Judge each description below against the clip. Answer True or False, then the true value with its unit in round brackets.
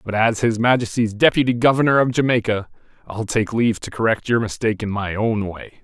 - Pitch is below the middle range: True (115 Hz)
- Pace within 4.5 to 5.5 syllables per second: False (5.9 syllables/s)